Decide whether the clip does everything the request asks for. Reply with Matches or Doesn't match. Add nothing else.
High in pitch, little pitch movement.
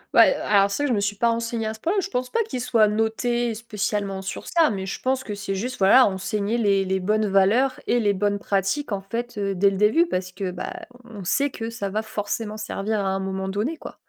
Doesn't match